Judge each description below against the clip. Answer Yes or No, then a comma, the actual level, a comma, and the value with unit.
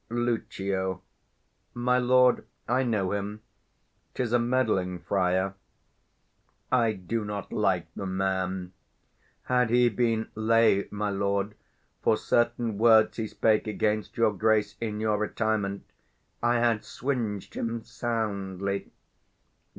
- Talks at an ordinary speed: No, slow, 115 wpm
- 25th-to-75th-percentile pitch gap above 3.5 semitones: No, average, 3.0 semitones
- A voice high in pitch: No, low, 110 Hz